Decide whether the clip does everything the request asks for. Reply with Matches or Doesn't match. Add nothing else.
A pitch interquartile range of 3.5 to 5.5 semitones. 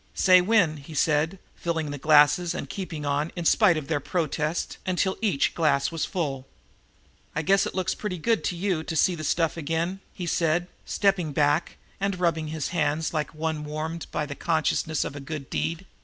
Doesn't match